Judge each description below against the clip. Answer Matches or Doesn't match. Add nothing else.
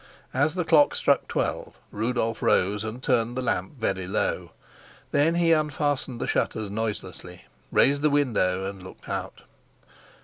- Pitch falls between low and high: Doesn't match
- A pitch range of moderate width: Doesn't match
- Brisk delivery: Doesn't match